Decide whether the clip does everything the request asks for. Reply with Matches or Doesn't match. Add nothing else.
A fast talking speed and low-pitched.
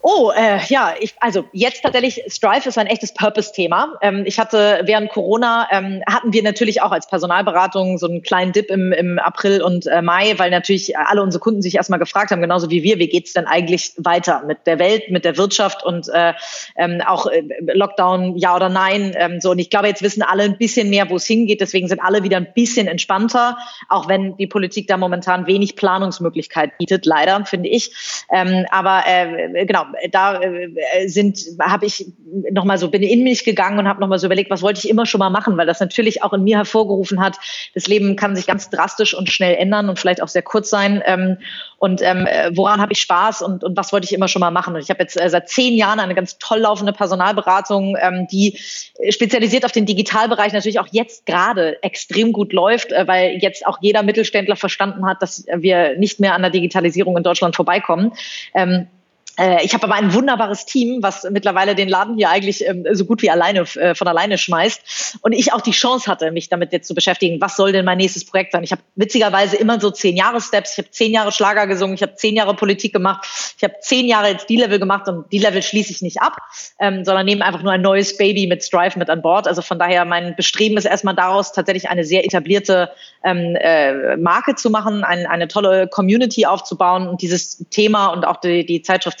Doesn't match